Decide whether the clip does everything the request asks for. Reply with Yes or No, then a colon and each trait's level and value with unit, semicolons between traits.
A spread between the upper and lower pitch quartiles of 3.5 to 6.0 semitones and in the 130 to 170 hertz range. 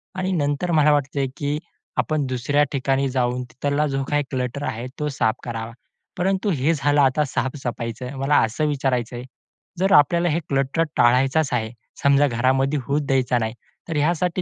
No: average, 2.8 semitones; medium, 140 Hz